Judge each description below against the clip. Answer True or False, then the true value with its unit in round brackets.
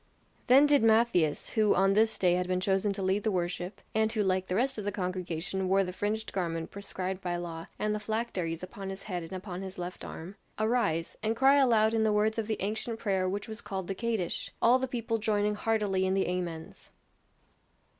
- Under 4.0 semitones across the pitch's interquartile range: True (3.1 semitones)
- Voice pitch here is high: True (195 Hz)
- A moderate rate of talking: False (215 wpm)